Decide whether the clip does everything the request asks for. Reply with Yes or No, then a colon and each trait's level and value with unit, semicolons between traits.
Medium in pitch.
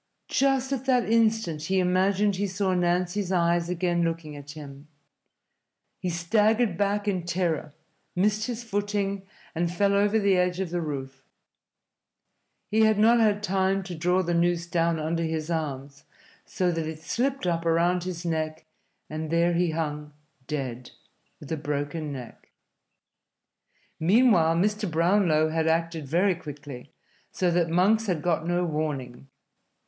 Yes: medium, 175 Hz